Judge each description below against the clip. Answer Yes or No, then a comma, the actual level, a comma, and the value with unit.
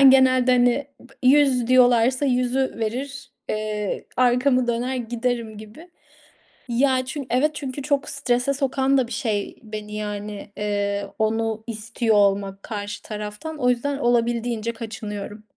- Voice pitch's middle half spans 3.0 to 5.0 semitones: Yes, average, 3.4 semitones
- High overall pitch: Yes, high, 240 Hz